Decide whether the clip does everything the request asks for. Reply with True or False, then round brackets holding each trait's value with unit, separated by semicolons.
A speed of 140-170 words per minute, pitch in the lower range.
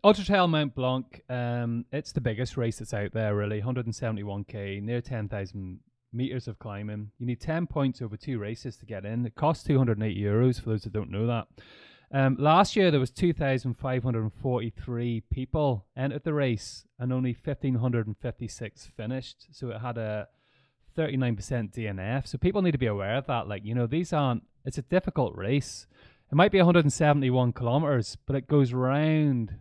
False (205 wpm; 125 Hz)